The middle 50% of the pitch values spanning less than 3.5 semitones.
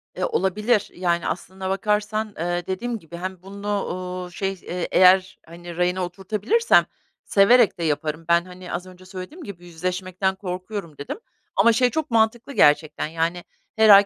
Yes: average, 2.9 semitones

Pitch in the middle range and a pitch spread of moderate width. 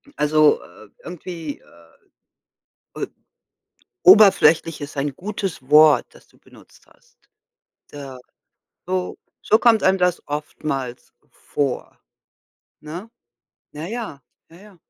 Yes: medium, 155 Hz; average, 4.4 semitones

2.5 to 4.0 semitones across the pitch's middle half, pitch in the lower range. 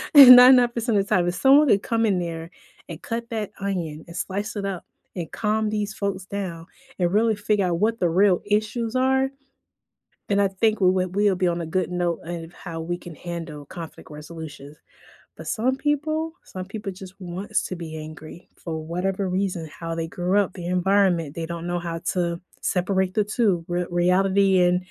No: average, 3.4 semitones; medium, 185 Hz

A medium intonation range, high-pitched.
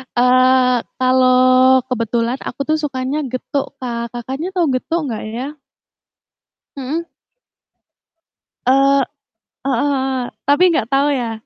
No: narrow, 1.9 semitones; very high, 260 Hz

